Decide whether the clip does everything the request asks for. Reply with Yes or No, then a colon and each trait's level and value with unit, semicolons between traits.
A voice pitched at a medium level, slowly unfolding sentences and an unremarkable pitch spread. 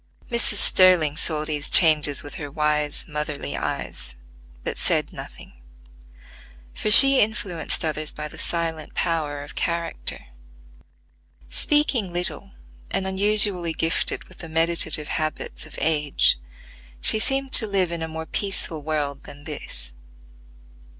Yes: medium, 160 Hz; slow, 130 wpm; average, 4.0 semitones